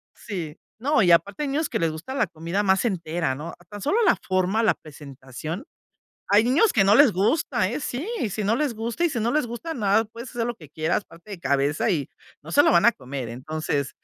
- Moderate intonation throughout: No, wide, 7.0 semitones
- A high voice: Yes, high, 195 Hz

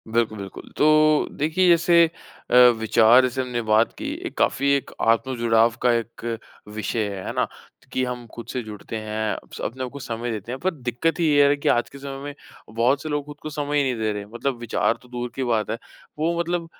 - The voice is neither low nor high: No, low, 125 Hz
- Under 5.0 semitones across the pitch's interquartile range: Yes, average, 4.2 semitones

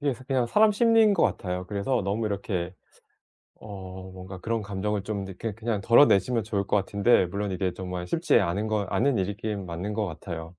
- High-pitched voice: No, low, 100 Hz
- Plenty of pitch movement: No, average, 3.6 semitones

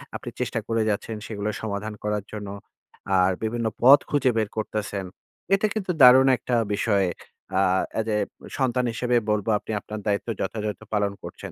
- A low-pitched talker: Yes, low, 110 Hz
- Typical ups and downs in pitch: Yes, average, 3.2 semitones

